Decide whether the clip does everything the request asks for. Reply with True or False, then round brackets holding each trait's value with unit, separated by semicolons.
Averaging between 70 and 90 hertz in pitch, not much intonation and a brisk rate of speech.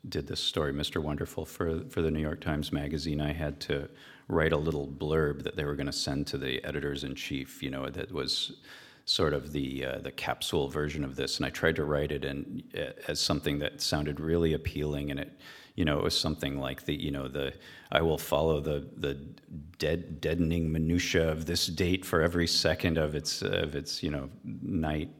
True (75 Hz; 2.1 semitones; 210 wpm)